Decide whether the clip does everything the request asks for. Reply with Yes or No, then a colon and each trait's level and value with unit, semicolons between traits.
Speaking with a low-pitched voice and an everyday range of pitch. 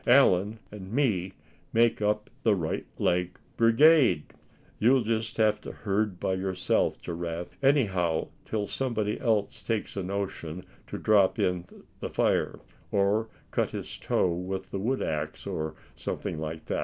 Yes: low, 100 Hz; average, 3.8 semitones